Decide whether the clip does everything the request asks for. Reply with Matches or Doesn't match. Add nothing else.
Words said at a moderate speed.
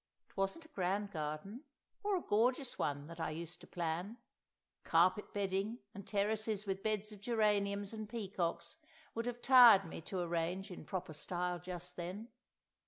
Matches